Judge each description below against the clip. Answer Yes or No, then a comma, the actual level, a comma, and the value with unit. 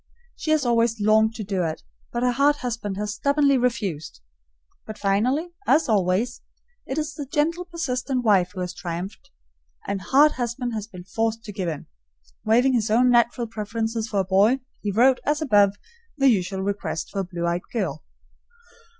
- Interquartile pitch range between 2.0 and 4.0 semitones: No, average, 4.5 semitones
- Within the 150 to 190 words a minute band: Yes, average, 175 wpm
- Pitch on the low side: No, high, 225 Hz